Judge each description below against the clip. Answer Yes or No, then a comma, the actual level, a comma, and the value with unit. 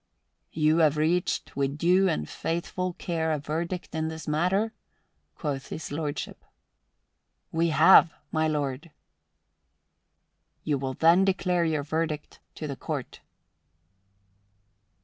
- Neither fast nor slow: No, slow, 115 wpm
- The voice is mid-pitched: Yes, medium, 160 Hz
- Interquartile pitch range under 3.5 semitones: Yes, narrow, 2.4 semitones